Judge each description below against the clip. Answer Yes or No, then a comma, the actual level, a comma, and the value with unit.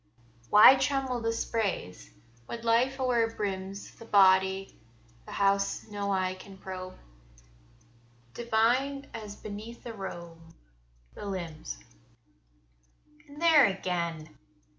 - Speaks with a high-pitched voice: Yes, high, 200 Hz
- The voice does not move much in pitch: No, average, 3.8 semitones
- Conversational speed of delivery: No, slow, 105 wpm